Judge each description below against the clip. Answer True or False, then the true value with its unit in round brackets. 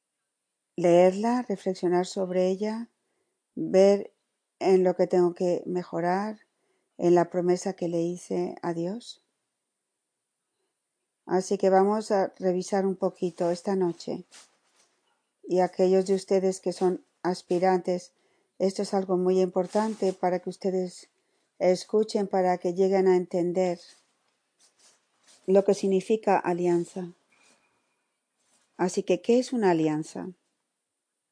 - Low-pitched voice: False (185 Hz)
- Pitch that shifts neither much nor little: False (1.7 semitones)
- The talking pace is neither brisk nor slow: False (115 wpm)